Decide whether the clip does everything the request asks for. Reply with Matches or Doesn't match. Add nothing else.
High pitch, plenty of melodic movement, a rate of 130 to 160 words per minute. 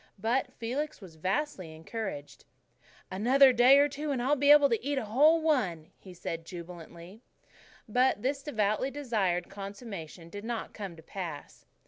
Matches